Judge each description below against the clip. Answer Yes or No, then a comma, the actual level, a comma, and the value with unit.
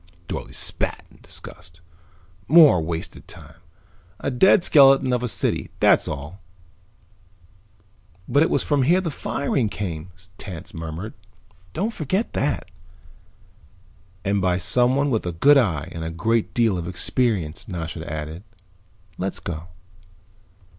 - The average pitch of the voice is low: Yes, low, 100 Hz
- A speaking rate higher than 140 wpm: No, slow, 135 wpm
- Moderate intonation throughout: No, wide, 8.6 semitones